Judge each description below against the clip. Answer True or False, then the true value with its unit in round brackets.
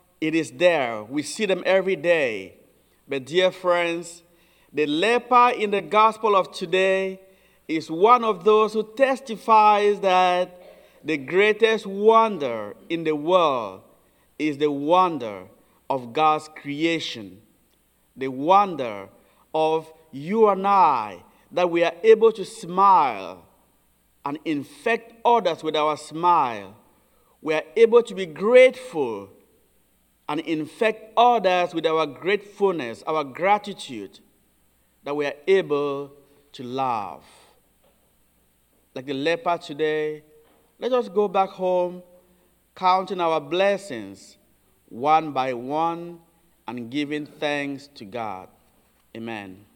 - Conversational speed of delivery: False (115 wpm)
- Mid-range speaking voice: True (170 Hz)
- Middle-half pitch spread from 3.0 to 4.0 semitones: False (5.0 semitones)